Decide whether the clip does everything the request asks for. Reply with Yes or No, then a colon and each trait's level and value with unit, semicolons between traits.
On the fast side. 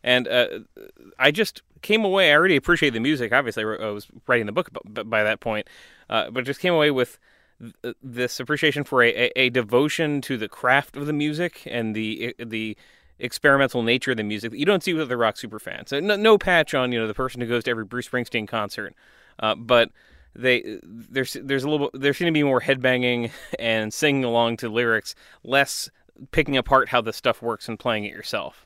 Yes: fast, 210 wpm